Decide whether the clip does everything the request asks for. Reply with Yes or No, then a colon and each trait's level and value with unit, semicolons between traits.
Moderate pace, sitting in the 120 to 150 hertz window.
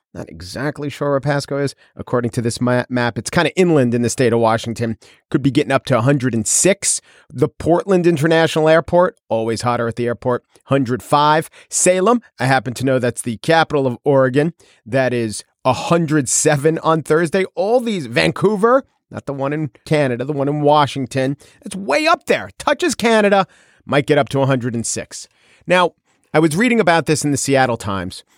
Yes: average, 175 wpm; medium, 140 Hz